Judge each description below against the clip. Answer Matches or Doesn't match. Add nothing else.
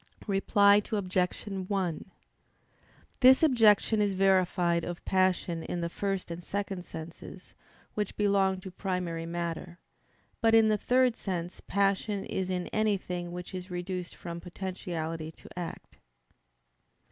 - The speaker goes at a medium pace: Doesn't match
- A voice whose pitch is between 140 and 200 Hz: Matches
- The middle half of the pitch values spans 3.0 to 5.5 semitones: Doesn't match